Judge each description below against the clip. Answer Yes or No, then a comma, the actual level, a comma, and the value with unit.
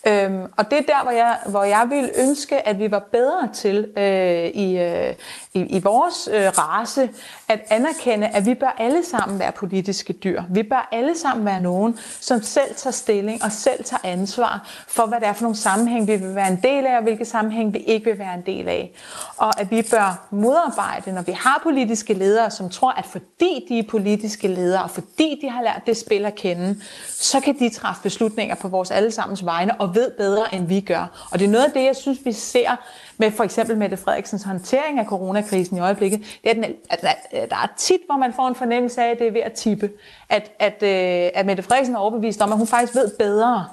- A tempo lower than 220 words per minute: No, fast, 225 wpm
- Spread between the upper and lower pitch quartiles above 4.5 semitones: No, average, 3.7 semitones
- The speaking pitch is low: No, high, 220 Hz